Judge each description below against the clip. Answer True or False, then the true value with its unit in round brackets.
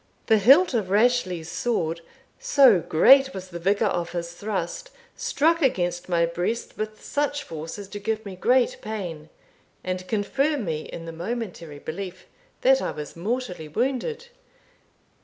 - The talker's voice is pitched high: True (200 Hz)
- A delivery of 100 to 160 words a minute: True (150 wpm)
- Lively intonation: True (6.4 semitones)